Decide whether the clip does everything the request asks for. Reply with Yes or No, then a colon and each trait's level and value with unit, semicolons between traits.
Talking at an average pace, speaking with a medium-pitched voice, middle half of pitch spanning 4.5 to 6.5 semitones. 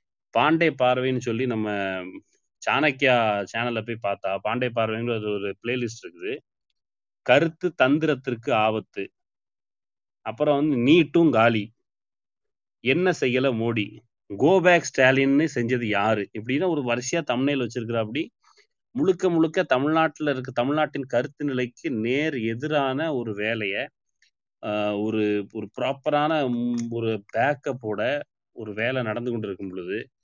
No: average, 105 wpm; low, 120 Hz; average, 5.3 semitones